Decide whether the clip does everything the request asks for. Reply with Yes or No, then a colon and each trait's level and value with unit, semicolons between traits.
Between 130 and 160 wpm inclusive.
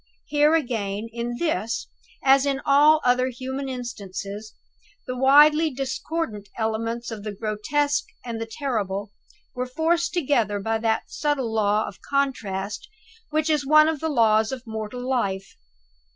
Yes: average, 140 wpm